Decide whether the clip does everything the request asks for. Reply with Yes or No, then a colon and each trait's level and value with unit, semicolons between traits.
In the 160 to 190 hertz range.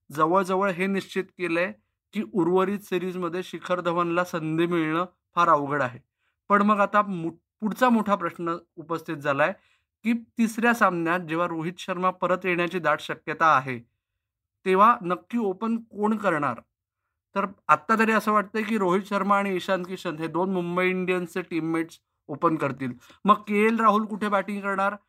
Yes: medium, 185 Hz